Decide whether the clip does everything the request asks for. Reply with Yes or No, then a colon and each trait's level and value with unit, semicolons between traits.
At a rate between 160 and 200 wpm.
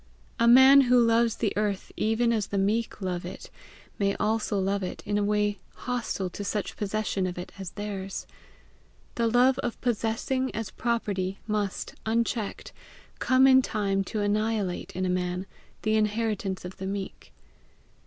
Yes: average, 165 wpm